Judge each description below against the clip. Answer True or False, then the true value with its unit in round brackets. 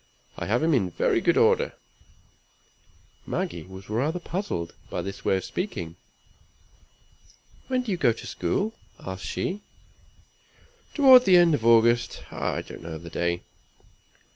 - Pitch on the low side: True (115 Hz)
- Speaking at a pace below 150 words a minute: True (140 wpm)